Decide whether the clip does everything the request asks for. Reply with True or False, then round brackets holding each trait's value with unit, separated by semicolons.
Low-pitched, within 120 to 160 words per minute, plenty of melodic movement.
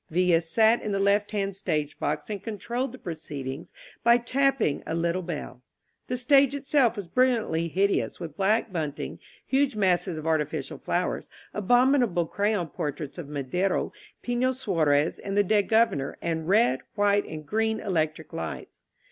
False (195 Hz; 155 wpm; 6.1 semitones)